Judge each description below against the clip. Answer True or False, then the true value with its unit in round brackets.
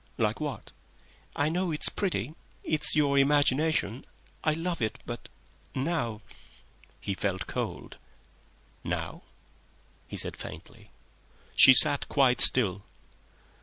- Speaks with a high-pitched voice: False (140 Hz)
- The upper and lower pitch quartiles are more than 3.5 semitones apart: True (4.7 semitones)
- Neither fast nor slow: False (105 wpm)